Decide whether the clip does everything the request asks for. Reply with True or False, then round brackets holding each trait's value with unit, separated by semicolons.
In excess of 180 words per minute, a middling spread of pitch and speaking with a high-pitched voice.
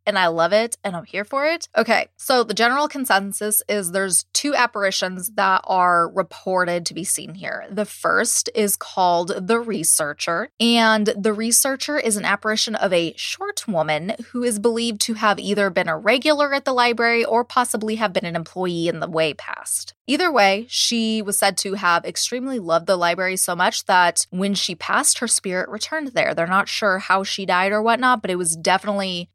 True (195 wpm; 4.2 semitones; 205 Hz)